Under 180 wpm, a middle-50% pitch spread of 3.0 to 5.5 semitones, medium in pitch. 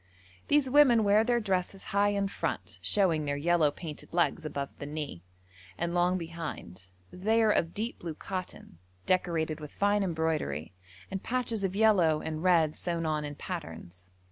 Yes: average, 165 wpm; average, 4.6 semitones; medium, 175 Hz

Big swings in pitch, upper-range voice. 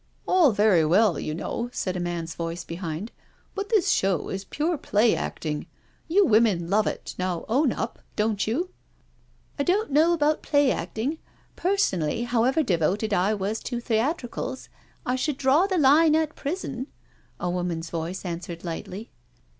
Yes: wide, 8.6 semitones; high, 225 Hz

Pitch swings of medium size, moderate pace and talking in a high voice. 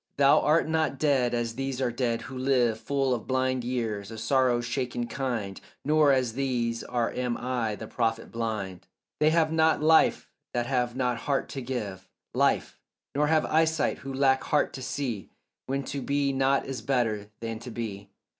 No: average, 3.0 semitones; average, 180 wpm; low, 125 Hz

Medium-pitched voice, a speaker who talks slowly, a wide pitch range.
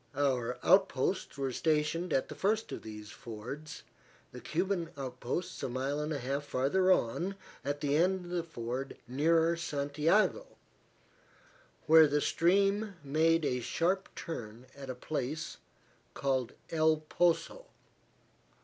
No: medium, 150 Hz; slow, 120 wpm; average, 4.7 semitones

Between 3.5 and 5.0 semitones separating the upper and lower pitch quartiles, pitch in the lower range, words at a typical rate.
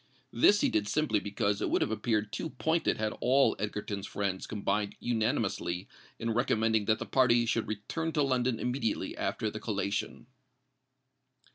No: average, 3.1 semitones; low, 110 Hz; average, 155 wpm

